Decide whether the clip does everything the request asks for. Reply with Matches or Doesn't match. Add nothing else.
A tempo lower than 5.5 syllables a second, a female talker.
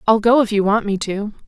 Doesn't match